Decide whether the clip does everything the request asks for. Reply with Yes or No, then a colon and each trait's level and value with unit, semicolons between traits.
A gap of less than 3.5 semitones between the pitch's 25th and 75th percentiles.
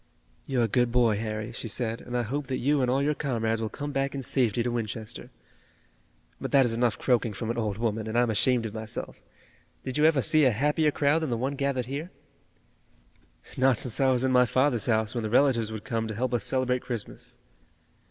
Yes: average, 3.0 semitones